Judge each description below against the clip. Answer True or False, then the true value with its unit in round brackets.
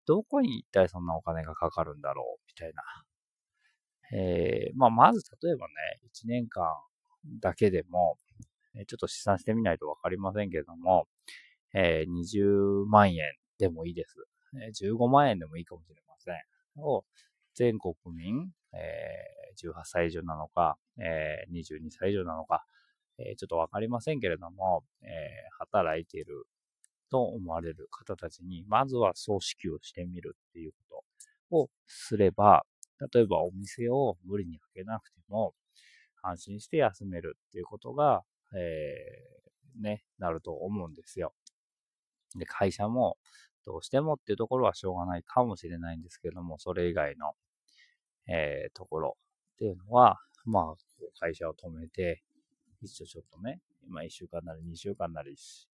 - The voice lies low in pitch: True (100 Hz)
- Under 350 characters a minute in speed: True (290 characters per minute)